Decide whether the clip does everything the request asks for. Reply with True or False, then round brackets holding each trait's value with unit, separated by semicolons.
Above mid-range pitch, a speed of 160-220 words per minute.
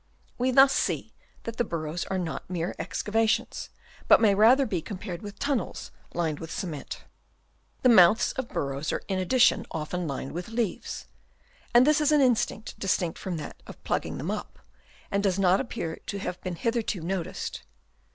True (195 Hz; 175 wpm)